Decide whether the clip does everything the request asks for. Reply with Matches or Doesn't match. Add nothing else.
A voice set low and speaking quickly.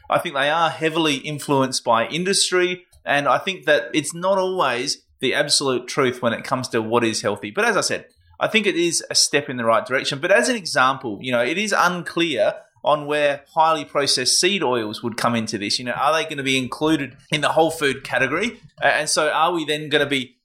Doesn't match